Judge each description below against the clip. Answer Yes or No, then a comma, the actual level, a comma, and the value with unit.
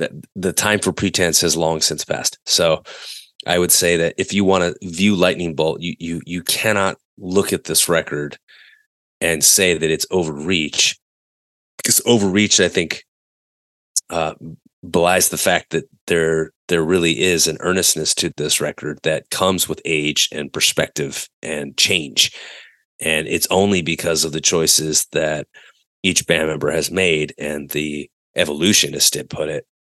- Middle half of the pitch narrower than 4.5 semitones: Yes, average, 3.4 semitones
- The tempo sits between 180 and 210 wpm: No, average, 155 wpm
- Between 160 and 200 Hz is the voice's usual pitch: No, very low, 85 Hz